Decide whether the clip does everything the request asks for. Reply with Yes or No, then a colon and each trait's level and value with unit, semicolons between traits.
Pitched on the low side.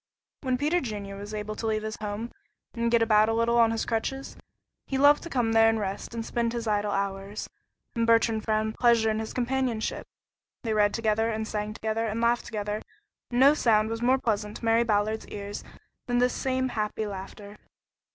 No: high, 225 Hz